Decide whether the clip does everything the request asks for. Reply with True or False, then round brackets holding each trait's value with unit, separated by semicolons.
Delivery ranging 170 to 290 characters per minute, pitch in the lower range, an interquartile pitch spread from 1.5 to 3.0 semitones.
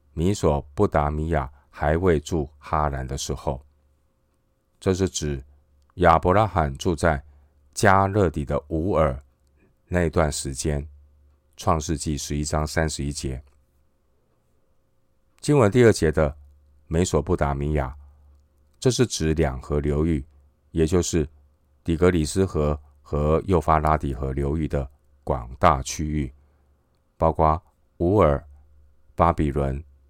True (180 characters per minute; 75 Hz; 2.4 semitones)